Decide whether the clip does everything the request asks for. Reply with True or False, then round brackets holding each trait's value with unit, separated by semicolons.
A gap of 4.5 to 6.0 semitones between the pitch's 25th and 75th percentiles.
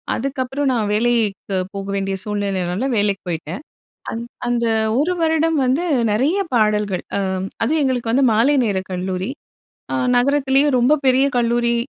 True (4.9 semitones)